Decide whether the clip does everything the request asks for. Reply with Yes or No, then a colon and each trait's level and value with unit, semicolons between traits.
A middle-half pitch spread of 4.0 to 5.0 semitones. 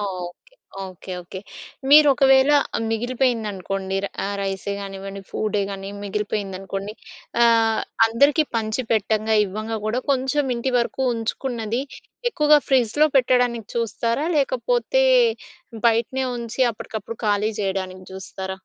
Yes: average, 4.6 semitones